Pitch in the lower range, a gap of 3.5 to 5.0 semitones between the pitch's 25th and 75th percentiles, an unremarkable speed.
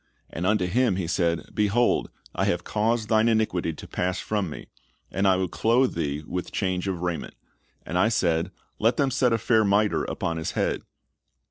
Yes: very low, 95 Hz; average, 4.0 semitones; average, 190 wpm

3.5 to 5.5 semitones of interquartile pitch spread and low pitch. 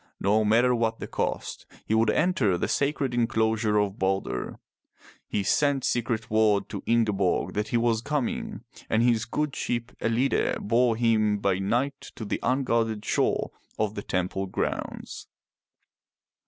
No: narrow, 2.6 semitones; low, 115 Hz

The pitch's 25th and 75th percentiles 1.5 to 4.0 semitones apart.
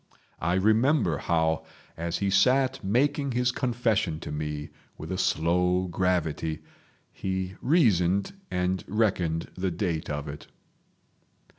No: average, 5.2 semitones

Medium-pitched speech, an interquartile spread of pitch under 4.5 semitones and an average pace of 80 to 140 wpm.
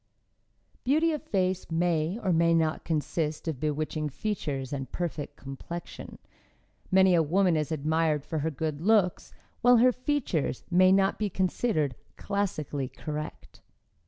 Yes: medium, 165 Hz; average, 4.0 semitones; slow, 135 wpm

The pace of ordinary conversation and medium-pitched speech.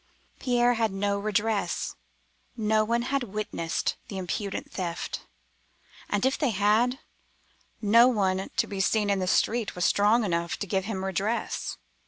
No: average, 150 wpm; high, 205 Hz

